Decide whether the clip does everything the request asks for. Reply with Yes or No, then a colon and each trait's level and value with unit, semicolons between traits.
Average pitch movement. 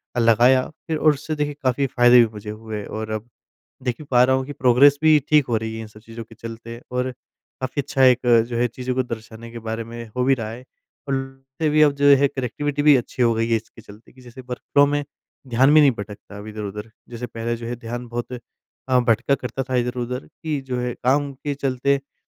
Yes: average, 3.0 semitones